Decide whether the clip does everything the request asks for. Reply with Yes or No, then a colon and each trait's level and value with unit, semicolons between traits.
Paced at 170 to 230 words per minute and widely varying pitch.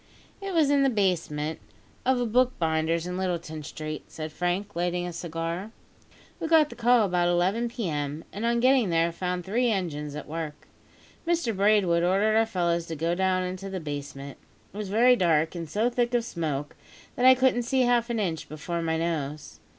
Yes: average, 190 wpm; wide, 6.1 semitones